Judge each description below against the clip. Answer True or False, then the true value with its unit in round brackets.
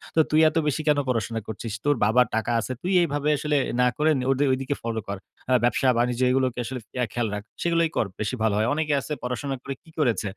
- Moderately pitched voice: False (130 Hz)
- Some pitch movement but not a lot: True (4.2 semitones)